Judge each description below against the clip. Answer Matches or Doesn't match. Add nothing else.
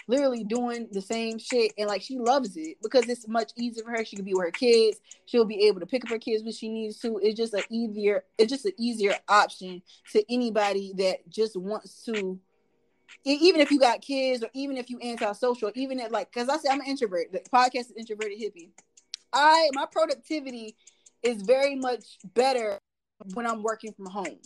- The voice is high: Matches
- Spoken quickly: Matches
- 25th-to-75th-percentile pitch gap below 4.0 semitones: Matches